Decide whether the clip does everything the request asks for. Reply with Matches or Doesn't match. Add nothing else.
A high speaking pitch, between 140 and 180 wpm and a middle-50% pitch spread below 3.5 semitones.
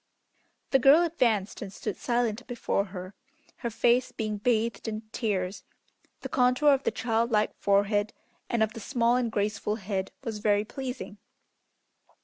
Matches